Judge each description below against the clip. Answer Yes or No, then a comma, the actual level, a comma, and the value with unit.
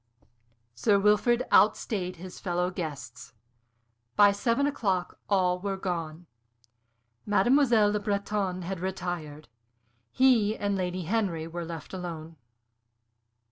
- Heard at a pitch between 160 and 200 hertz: Yes, medium, 185 Hz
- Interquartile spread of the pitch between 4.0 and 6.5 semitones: No, average, 3.1 semitones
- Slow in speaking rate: Yes, slow, 105 wpm